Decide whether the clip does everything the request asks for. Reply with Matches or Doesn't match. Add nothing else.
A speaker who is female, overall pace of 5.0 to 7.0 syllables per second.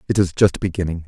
Doesn't match